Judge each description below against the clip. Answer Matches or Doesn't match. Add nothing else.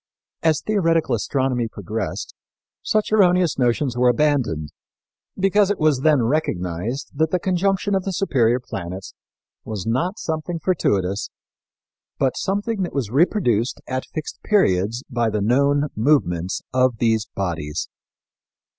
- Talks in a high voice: Doesn't match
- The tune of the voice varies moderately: Doesn't match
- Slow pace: Matches